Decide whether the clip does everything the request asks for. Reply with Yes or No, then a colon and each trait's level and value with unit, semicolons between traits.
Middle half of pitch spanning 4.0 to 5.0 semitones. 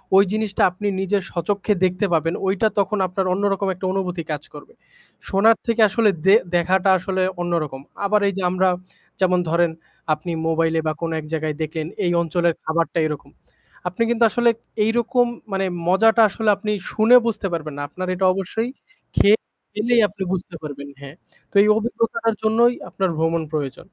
Yes: average, 4.3 semitones